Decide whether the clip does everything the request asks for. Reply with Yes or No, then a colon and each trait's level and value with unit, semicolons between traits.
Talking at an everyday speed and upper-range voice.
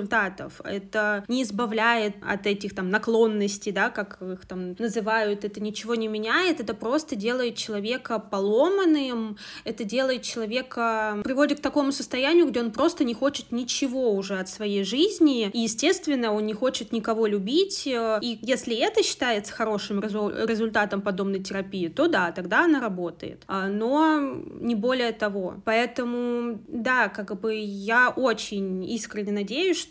Yes: average, 145 wpm; high, 225 Hz